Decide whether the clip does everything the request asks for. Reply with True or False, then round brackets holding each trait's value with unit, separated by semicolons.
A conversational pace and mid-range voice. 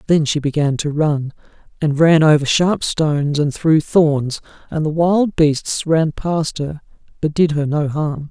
True (180 wpm; 155 Hz)